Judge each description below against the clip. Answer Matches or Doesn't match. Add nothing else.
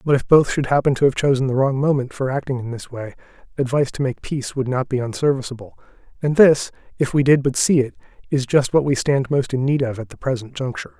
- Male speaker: Matches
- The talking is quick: Matches